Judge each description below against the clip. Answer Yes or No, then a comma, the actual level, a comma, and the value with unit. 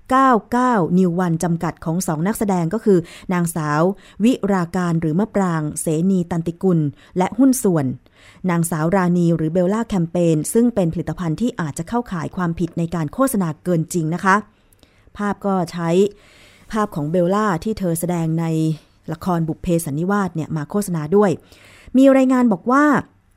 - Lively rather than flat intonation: No, average, 4.0 semitones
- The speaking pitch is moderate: Yes, medium, 175 Hz